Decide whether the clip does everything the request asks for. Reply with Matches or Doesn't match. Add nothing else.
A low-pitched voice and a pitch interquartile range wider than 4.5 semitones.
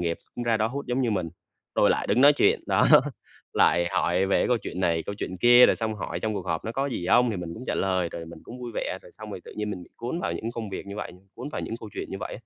Matches